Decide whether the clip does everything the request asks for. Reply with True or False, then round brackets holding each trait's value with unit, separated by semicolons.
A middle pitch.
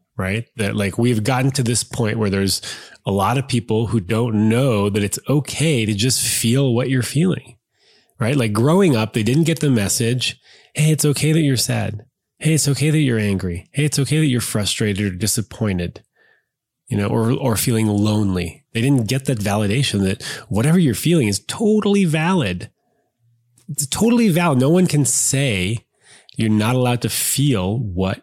False (120 Hz)